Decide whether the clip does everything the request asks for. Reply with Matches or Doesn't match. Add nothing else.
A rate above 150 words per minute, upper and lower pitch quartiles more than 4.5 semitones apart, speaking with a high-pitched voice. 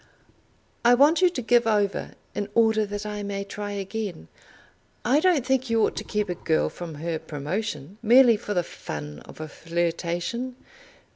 Matches